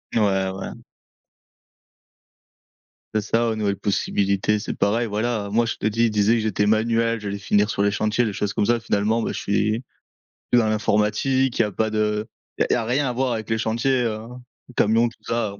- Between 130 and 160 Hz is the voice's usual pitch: No, low, 110 Hz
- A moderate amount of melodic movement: No, narrow, 2.0 semitones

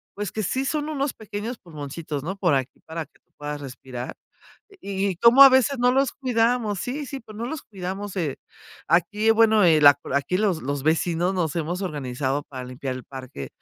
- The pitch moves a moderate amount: No, wide, 7.7 semitones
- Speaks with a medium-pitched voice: Yes, medium, 180 Hz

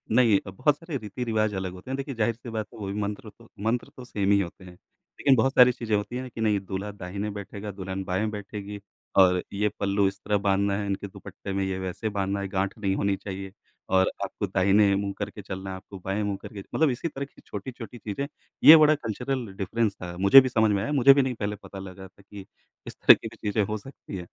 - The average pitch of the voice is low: Yes, low, 100 Hz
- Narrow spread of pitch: No, average, 3.1 semitones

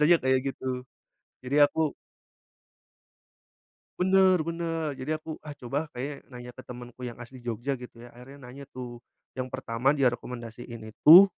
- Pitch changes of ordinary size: Yes, average, 3.6 semitones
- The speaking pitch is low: Yes, low, 130 Hz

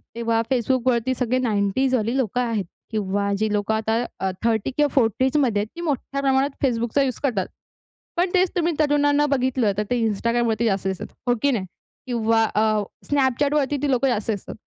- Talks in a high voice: Yes, high, 240 Hz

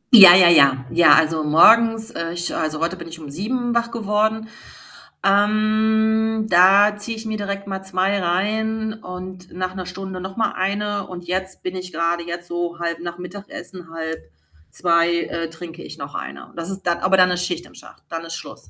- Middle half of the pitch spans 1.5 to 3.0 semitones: No, average, 3.5 semitones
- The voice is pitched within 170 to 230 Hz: Yes, medium, 185 Hz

